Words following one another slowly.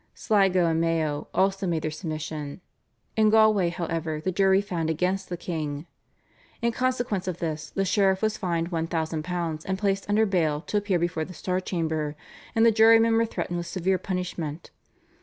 No: average, 170 wpm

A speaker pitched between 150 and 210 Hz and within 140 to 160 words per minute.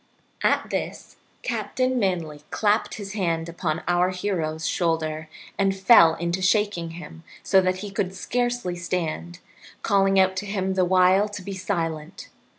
Yes: medium, 185 Hz; average, 150 wpm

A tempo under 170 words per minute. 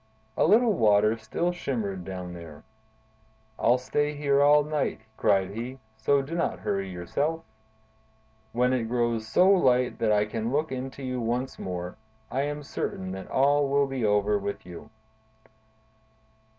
Yes: average, 150 wpm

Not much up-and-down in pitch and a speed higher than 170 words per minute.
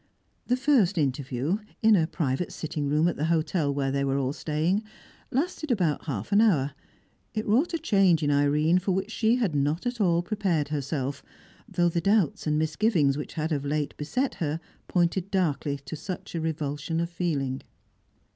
No: average, 5.0 semitones; average, 180 wpm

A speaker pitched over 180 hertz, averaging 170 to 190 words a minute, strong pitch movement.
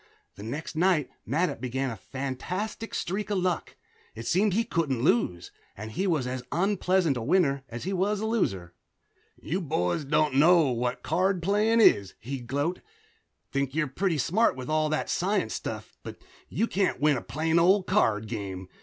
No: medium, 155 Hz; average, 175 wpm; wide, 6.7 semitones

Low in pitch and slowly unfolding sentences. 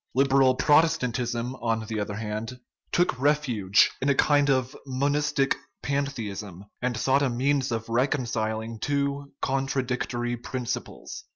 Yes: low, 130 Hz; slow, 125 wpm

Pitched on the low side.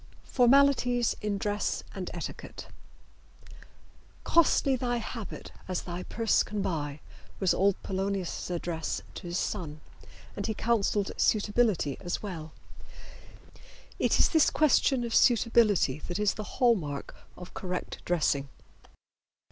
No: high, 205 Hz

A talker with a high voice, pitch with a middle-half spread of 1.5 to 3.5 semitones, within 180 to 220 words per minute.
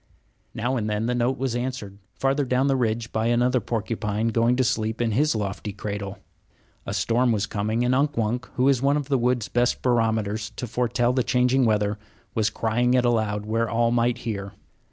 No: low, 115 Hz; narrow, 2.4 semitones; average, 195 wpm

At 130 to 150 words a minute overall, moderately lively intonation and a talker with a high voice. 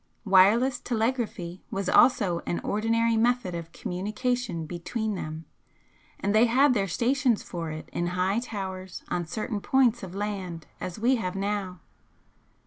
Yes: average, 140 wpm; average, 4.5 semitones; high, 205 Hz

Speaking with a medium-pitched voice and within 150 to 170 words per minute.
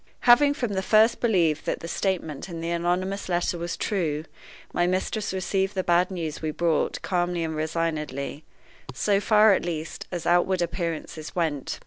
Yes: medium, 175 Hz; average, 165 wpm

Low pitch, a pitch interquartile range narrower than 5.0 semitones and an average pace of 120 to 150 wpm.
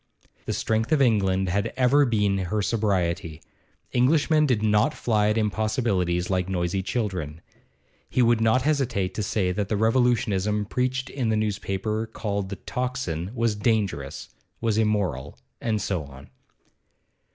Yes: low, 105 Hz; average, 3.5 semitones; average, 140 wpm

